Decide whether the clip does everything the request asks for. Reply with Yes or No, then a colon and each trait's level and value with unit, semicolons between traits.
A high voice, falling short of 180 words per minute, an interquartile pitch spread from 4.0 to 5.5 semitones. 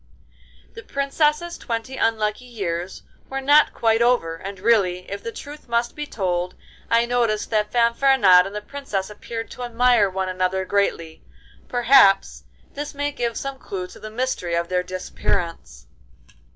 Yes: high, 225 Hz; average, 150 wpm; average, 5.0 semitones